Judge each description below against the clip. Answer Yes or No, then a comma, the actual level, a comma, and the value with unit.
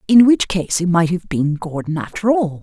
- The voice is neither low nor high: Yes, medium, 180 Hz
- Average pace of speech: No, fast, 230 wpm